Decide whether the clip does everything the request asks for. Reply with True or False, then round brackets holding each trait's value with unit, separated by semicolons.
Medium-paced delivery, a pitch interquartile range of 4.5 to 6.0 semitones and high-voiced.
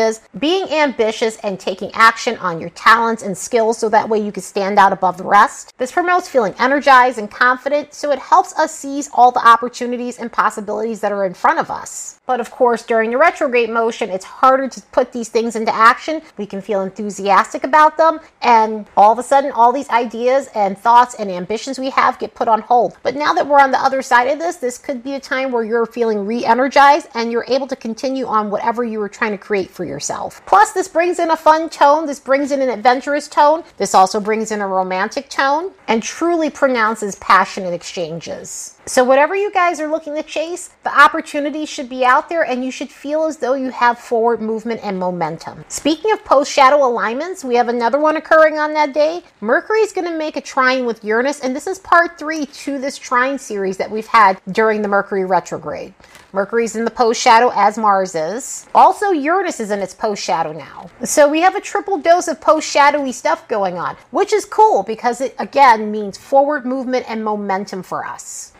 False (215 wpm; 5.3 semitones; 245 Hz)